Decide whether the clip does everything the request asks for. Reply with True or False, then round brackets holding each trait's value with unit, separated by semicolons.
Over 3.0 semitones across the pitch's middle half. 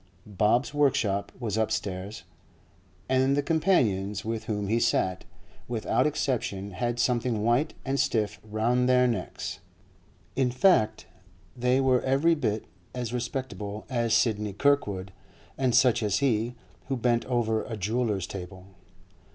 True (3.6 semitones)